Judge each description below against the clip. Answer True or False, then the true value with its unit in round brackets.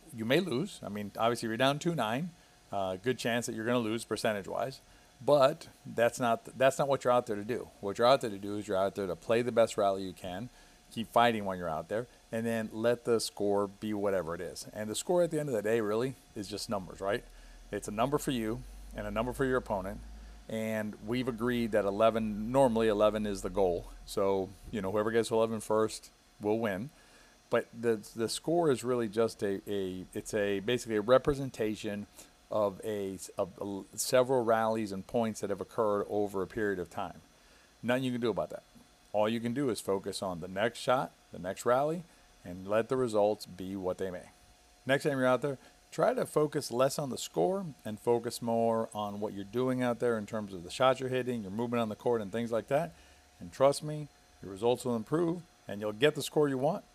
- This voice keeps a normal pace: False (225 wpm)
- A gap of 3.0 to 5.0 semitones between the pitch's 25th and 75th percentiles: True (3.5 semitones)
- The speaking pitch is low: True (115 Hz)